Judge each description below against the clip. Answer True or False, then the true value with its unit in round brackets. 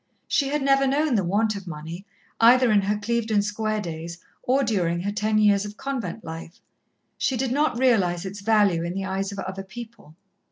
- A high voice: True (210 Hz)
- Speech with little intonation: False (3.8 semitones)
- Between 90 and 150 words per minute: False (195 wpm)